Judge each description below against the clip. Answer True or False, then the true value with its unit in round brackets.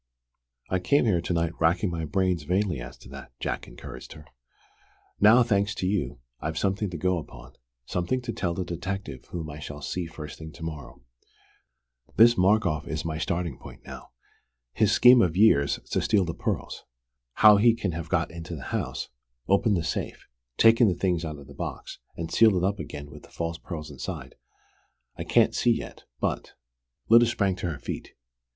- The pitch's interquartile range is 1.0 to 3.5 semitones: False (4.3 semitones)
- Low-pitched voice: True (85 Hz)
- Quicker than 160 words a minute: True (190 wpm)